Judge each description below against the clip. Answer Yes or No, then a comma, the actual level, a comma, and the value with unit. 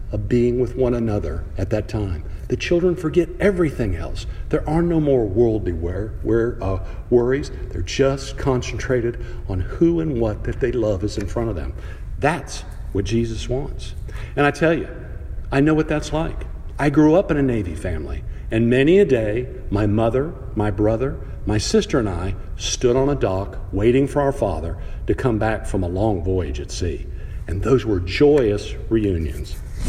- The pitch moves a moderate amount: No, wide, 5.8 semitones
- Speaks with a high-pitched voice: No, low, 110 Hz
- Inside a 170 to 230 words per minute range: Yes, average, 180 wpm